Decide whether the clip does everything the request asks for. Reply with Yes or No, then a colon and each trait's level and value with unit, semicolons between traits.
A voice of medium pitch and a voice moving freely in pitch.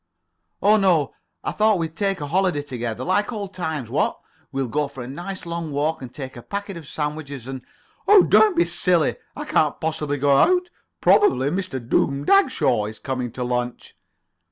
Yes: medium, 150 Hz; wide, 6.6 semitones